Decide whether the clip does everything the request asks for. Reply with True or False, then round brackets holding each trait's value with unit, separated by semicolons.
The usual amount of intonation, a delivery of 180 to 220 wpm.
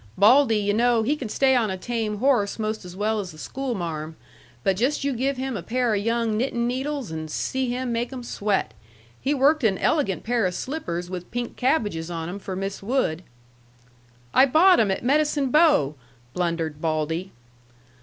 False (5.9 semitones; 185 wpm)